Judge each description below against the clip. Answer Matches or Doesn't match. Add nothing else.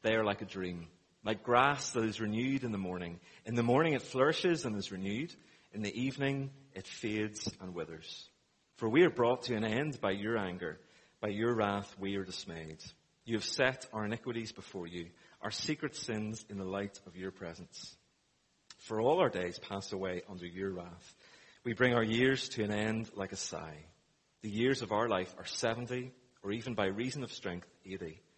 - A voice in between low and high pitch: Doesn't match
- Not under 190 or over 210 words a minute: Matches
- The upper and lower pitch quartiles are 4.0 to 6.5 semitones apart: Matches